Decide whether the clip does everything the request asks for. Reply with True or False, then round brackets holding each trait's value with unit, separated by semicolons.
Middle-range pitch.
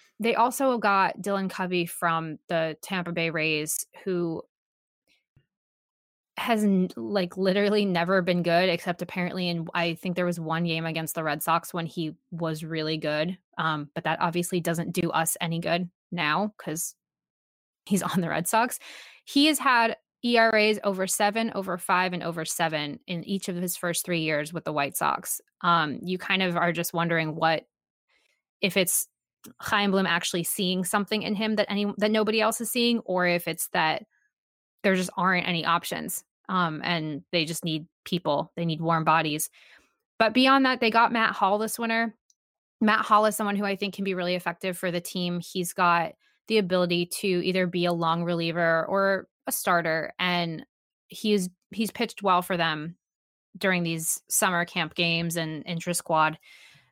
True (180 Hz)